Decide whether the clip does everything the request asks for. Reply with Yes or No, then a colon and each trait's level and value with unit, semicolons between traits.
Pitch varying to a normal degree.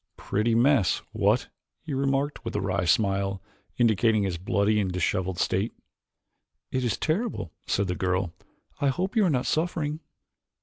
No: wide, 6.5 semitones